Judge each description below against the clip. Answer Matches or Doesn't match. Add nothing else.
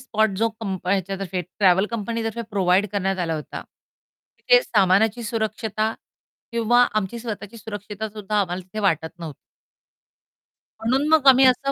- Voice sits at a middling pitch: Doesn't match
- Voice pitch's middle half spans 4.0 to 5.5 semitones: Doesn't match